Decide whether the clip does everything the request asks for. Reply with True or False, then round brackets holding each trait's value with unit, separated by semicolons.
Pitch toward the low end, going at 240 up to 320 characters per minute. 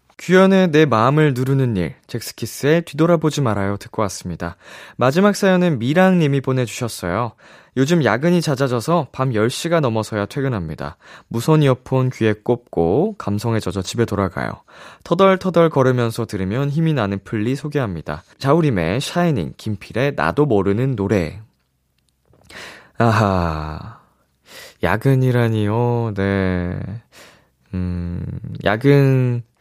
True (120 Hz; 280 characters per minute)